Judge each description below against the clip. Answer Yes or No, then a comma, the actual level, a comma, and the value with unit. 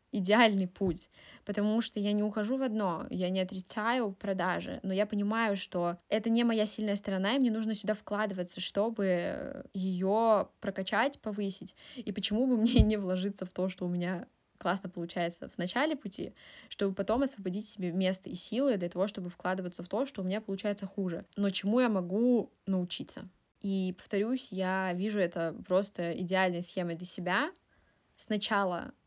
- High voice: Yes, high, 200 Hz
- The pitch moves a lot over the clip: No, average, 2.7 semitones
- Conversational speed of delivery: No, fast, 165 wpm